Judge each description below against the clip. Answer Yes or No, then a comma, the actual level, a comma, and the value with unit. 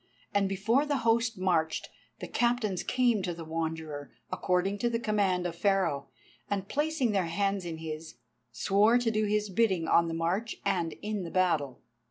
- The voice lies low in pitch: No, high, 195 Hz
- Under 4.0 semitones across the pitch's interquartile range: No, average, 4.8 semitones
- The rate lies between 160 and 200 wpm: Yes, average, 175 wpm